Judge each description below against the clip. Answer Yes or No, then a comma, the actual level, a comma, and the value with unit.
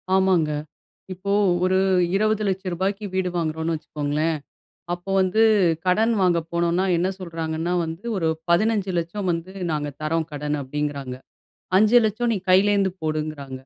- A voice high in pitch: No, medium, 175 Hz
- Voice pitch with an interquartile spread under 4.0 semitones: Yes, average, 3.6 semitones